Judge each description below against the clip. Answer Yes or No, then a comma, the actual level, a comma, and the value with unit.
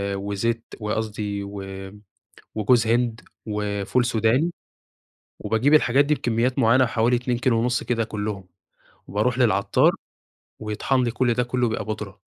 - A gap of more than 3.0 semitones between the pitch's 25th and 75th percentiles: No, average, 2.7 semitones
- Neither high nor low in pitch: No, low, 115 Hz